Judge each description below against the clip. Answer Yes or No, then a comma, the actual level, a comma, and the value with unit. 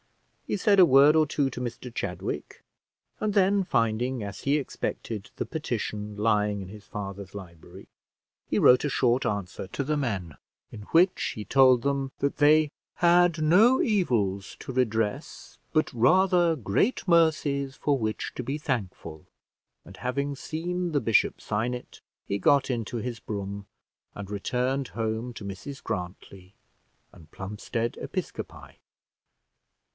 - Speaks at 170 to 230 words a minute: No, average, 145 wpm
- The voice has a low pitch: Yes, low, 125 Hz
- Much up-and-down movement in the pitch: Yes, wide, 6.4 semitones